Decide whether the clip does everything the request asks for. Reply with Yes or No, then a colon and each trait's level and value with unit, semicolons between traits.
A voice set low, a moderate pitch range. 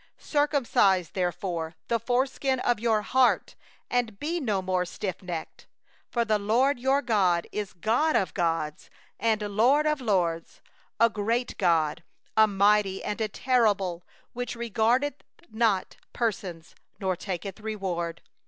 No: high, 210 Hz; average, 4.6 semitones